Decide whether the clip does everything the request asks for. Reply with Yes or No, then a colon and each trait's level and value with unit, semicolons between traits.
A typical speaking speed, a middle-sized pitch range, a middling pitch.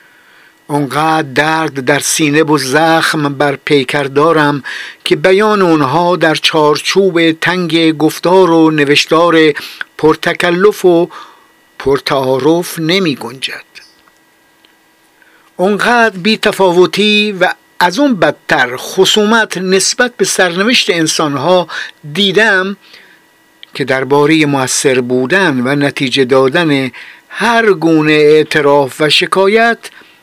No: slow, 95 wpm; average, 4.5 semitones; medium, 165 Hz